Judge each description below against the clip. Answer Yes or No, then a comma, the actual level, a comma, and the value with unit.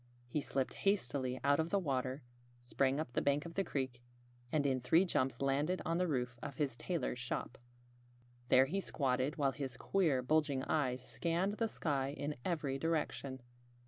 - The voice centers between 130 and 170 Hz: Yes, medium, 140 Hz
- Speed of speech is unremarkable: Yes, average, 175 wpm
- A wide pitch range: No, average, 3.7 semitones